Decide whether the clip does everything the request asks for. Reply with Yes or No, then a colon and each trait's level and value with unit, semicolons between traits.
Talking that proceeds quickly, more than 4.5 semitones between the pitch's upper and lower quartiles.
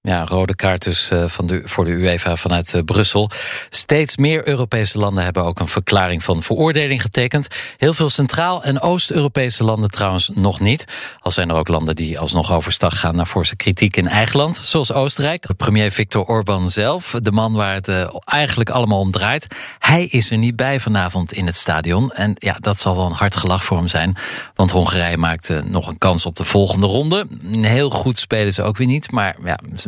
Yes: fast, 205 wpm; wide, 5.5 semitones